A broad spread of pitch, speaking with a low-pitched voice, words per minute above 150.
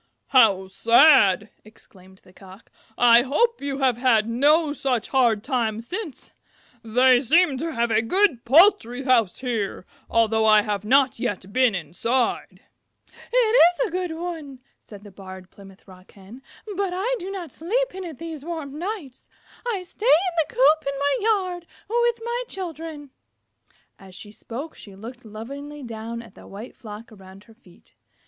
No: wide, 7.2 semitones; very high, 255 Hz; average, 165 wpm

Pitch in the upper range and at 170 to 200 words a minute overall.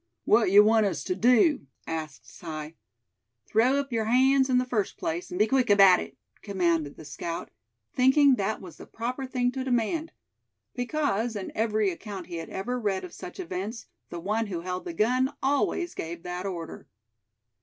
Yes: high, 215 Hz; average, 180 wpm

